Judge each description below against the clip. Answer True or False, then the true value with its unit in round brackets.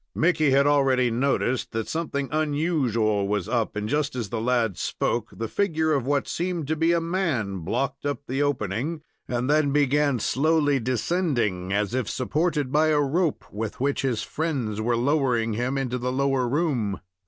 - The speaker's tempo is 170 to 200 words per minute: True (175 wpm)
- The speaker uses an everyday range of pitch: True (4.5 semitones)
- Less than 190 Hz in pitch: True (135 Hz)